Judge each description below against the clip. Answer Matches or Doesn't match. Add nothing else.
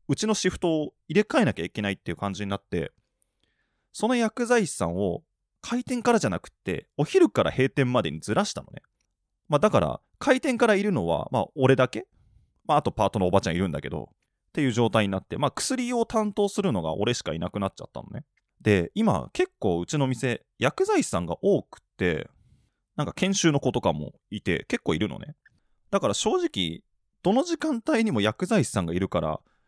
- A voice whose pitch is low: Doesn't match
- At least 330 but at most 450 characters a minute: Matches